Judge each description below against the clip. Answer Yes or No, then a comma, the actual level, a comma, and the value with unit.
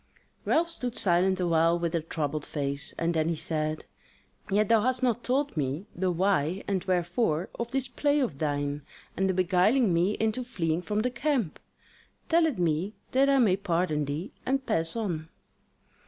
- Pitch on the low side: No, medium, 185 Hz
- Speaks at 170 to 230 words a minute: Yes, average, 175 wpm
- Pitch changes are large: Yes, wide, 6.6 semitones